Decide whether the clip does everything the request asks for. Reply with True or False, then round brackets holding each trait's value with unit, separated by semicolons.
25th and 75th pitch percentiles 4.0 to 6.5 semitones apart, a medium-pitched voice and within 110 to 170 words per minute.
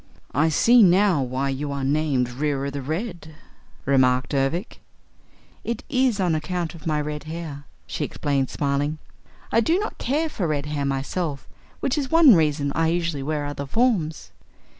True (4.4 semitones; 155 Hz; 160 wpm)